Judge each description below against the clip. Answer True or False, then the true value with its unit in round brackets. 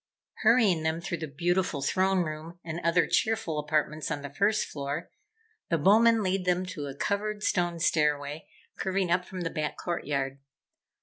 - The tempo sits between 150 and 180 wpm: True (165 wpm)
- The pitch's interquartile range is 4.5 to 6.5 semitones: False (3.8 semitones)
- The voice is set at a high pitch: False (170 Hz)